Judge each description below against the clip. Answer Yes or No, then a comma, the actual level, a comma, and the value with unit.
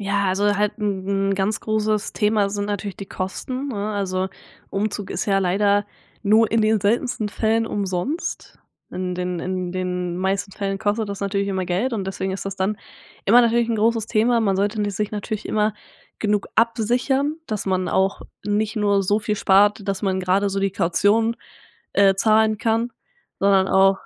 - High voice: Yes, high, 205 Hz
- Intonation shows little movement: Yes, narrow, 2.0 semitones